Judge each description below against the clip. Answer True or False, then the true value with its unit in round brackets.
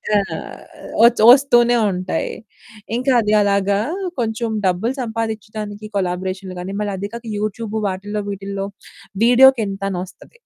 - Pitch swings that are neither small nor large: True (3.0 semitones)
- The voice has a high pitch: True (210 Hz)